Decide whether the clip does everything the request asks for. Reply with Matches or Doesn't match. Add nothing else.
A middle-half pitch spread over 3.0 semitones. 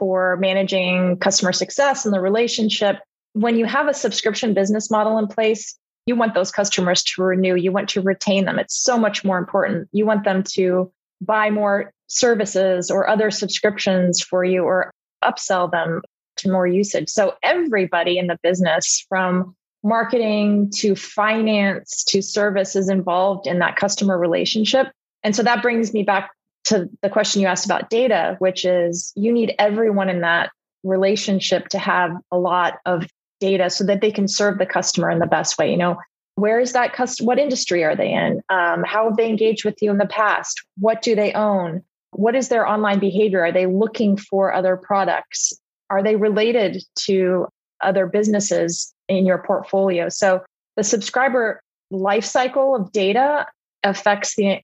Doesn't match